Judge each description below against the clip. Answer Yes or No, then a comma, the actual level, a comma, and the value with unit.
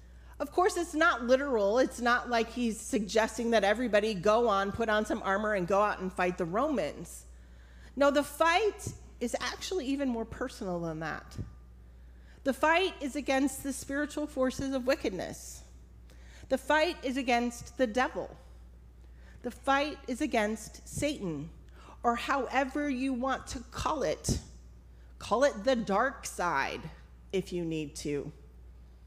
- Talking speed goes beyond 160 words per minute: No, average, 145 wpm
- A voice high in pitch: Yes, high, 230 Hz